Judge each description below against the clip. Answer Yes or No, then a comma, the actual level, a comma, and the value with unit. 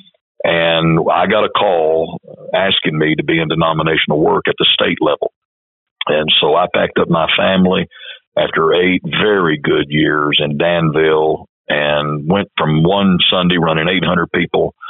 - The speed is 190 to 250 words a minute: No, average, 155 wpm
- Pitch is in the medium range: No, very low, 80 Hz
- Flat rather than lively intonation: Yes, narrow, 1.7 semitones